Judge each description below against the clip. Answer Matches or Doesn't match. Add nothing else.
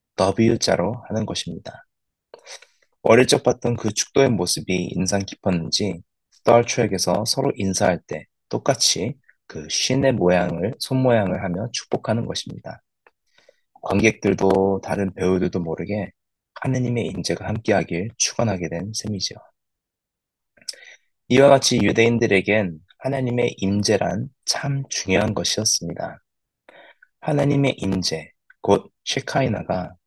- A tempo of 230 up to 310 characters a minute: Matches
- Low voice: Matches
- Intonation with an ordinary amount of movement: Matches